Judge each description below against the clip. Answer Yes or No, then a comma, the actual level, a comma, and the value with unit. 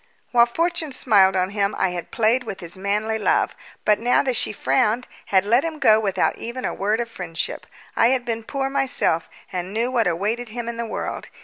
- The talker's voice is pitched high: Yes, high, 225 Hz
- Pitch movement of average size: Yes, average, 3.7 semitones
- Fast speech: Yes, fast, 210 wpm